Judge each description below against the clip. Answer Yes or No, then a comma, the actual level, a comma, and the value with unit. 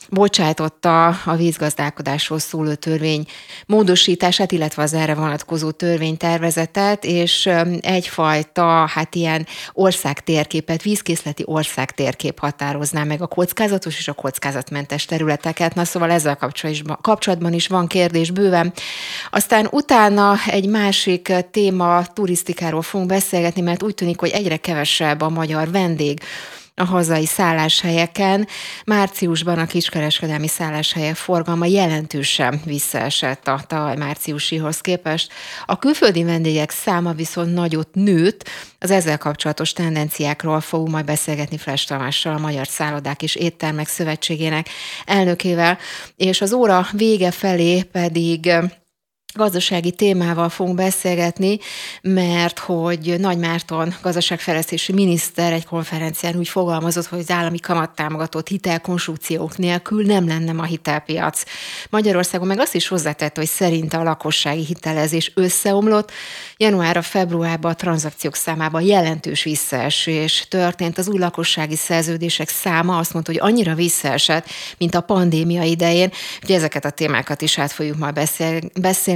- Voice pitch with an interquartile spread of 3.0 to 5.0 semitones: No, narrow, 2.6 semitones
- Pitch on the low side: No, medium, 170 Hz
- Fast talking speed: No, average, 125 wpm